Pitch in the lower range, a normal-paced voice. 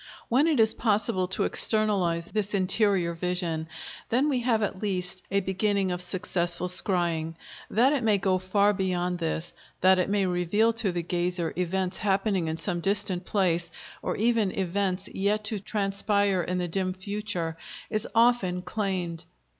No: high, 190 Hz; average, 160 wpm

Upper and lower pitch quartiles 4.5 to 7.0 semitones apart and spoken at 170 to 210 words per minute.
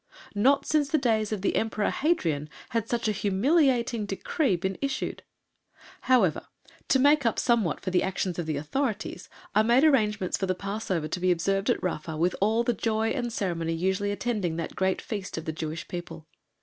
Yes: average, 4.8 semitones; average, 190 wpm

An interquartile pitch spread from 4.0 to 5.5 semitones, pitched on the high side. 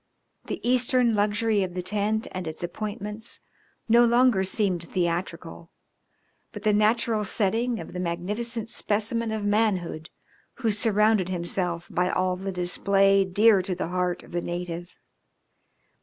No: average, 3.5 semitones; high, 200 Hz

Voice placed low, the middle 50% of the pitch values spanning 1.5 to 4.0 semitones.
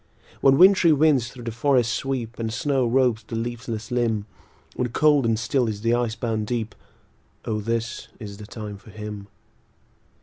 Yes: low, 115 Hz; narrow, 2.5 semitones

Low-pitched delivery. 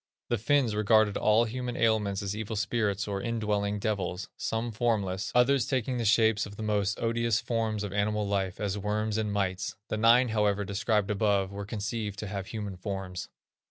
Yes: low, 105 Hz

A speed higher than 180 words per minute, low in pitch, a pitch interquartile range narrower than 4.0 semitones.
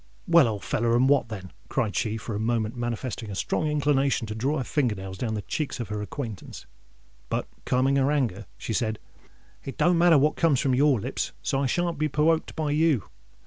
No: average, 200 wpm; low, 130 Hz; average, 5.1 semitones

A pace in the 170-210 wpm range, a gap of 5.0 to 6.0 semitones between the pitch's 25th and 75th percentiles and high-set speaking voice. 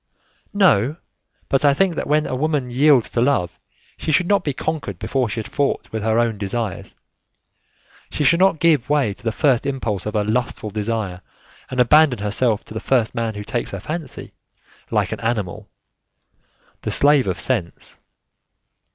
No: average, 175 wpm; average, 5.3 semitones; low, 125 Hz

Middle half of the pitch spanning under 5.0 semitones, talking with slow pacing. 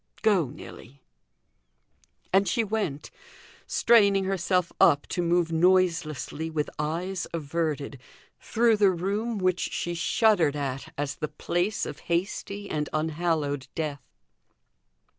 Yes: average, 4.3 semitones; slow, 115 wpm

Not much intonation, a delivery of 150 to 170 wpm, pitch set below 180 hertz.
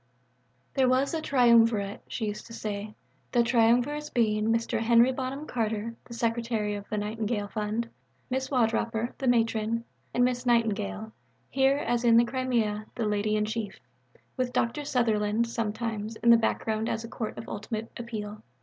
No: narrow, 2.2 semitones; average, 160 wpm; high, 230 Hz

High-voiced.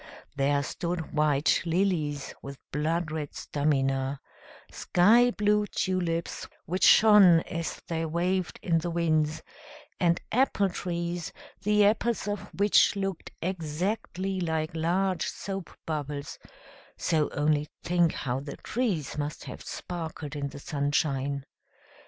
No: medium, 165 Hz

